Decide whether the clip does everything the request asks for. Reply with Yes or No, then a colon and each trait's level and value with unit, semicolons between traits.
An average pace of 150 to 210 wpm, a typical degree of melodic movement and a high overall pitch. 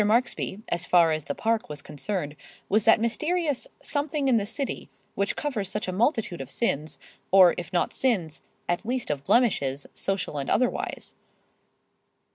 No: average, 160 wpm; wide, 6.7 semitones; high, 200 Hz